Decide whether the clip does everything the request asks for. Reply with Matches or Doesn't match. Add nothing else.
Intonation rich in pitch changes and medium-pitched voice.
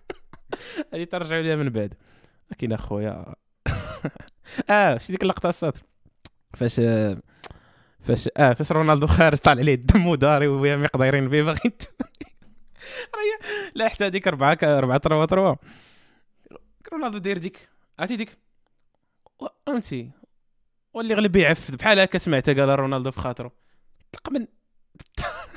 Matches